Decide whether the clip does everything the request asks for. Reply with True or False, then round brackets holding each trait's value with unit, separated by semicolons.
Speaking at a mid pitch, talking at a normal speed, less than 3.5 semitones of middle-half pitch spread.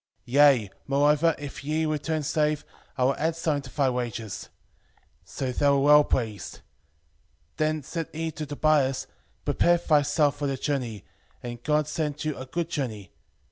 True (145 Hz; 165 wpm; 2.8 semitones)